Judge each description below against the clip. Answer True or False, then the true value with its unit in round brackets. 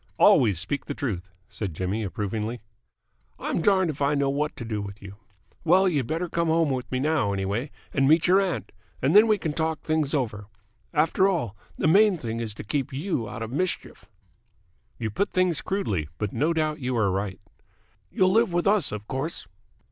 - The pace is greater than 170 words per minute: True (195 wpm)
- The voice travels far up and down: True (7.5 semitones)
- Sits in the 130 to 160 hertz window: True (140 Hz)